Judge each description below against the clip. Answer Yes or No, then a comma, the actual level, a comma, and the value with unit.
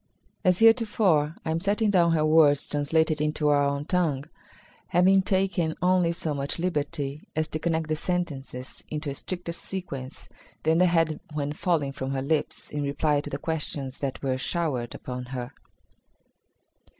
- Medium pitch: Yes, medium, 155 Hz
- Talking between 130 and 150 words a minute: No, average, 160 wpm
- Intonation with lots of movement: No, average, 3.5 semitones